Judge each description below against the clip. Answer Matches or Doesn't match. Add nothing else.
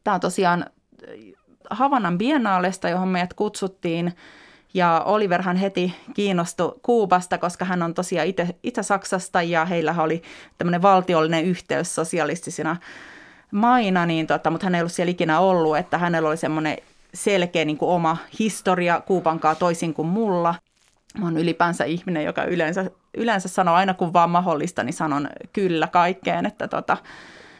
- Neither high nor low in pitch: Matches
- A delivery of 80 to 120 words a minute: Doesn't match